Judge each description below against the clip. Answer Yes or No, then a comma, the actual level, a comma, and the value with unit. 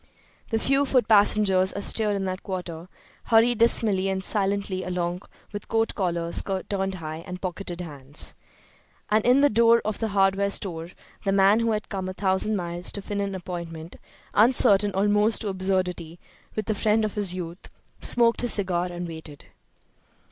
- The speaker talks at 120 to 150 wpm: No, average, 165 wpm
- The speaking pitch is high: Yes, high, 195 Hz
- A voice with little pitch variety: No, average, 3.0 semitones